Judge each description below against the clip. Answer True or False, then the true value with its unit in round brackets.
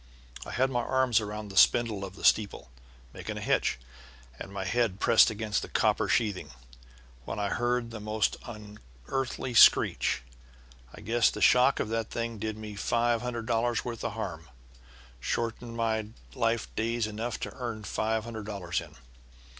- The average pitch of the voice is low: True (110 Hz)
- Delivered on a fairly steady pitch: True (2.2 semitones)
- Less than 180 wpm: True (165 wpm)